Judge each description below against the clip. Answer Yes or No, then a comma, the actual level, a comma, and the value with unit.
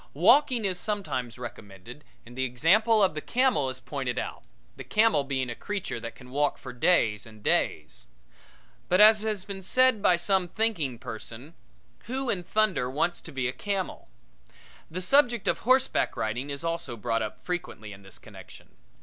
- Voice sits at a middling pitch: Yes, medium, 160 Hz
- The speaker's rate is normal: Yes, average, 175 wpm